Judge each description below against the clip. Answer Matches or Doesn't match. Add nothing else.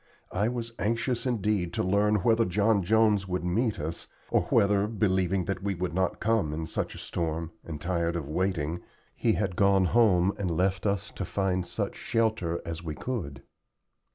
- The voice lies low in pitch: Matches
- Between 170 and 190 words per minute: Matches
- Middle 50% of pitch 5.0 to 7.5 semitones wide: Doesn't match